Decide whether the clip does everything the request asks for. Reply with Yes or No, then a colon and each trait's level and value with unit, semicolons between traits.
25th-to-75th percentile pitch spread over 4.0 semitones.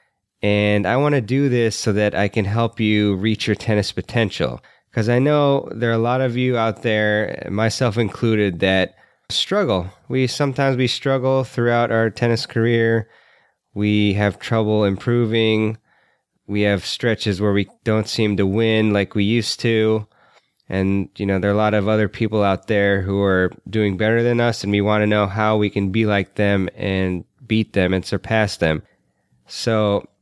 No: narrow, 2.4 semitones